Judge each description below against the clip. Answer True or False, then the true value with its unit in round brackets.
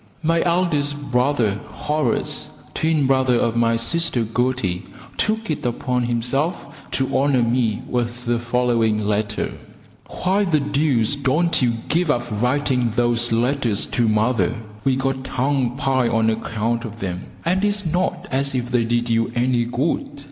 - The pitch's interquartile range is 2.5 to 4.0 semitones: True (3.6 semitones)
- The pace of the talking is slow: False (150 wpm)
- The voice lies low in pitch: True (125 Hz)